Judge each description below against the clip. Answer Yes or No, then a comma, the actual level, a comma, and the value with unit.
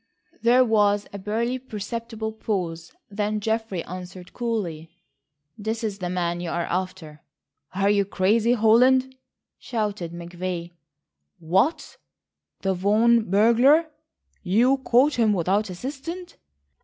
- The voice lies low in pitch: No, high, 210 Hz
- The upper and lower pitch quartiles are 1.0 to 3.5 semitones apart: No, average, 4.3 semitones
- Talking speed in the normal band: No, slow, 115 wpm